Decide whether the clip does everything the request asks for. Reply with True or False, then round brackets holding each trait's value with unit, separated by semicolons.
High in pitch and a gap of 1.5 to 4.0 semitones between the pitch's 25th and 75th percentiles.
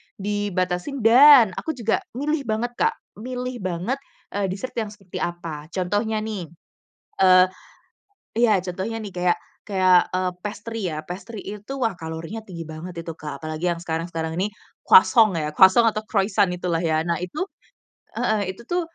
False (195 Hz; 4.4 semitones)